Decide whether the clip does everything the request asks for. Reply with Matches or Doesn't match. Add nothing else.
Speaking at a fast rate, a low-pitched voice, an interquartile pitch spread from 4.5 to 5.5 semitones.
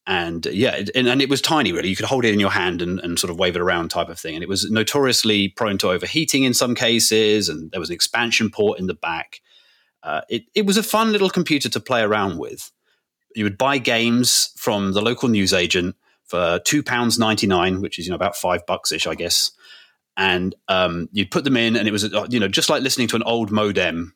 Matches